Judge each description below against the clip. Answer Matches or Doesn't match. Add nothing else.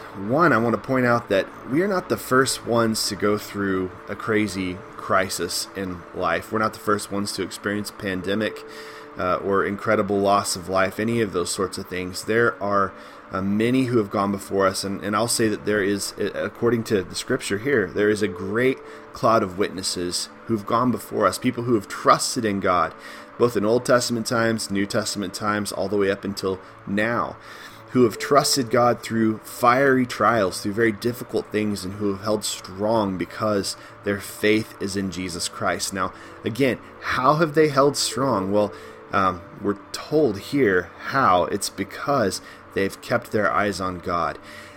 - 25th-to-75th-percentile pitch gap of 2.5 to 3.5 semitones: Matches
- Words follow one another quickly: Doesn't match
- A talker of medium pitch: Doesn't match